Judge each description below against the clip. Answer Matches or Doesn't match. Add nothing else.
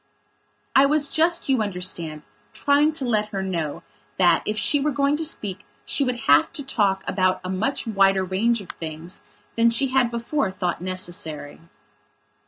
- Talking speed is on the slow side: Doesn't match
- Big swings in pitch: Matches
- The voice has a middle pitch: Doesn't match